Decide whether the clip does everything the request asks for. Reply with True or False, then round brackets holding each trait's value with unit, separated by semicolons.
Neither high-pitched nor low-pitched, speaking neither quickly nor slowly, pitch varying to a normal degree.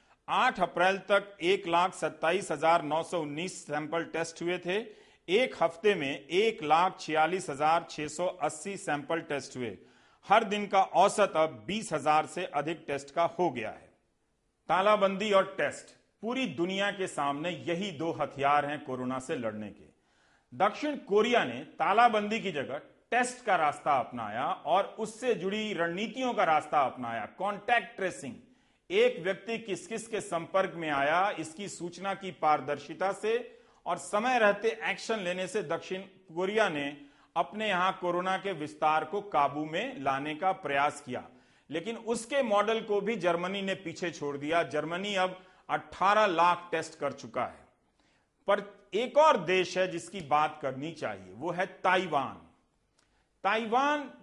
True (180 Hz; 155 wpm; 4.8 semitones)